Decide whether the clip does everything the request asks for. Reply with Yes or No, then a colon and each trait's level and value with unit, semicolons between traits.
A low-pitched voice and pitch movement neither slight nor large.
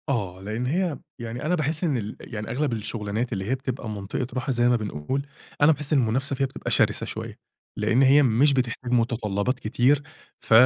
Yes: low, 125 Hz; average, 3.9 semitones